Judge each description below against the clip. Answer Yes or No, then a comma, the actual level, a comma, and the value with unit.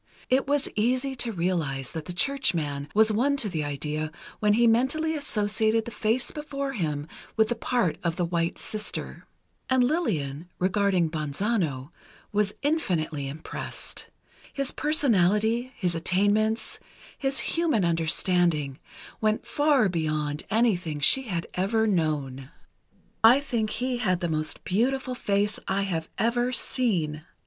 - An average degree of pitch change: No, wide, 6.9 semitones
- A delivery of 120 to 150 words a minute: Yes, slow, 135 wpm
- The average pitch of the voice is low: No, high, 205 Hz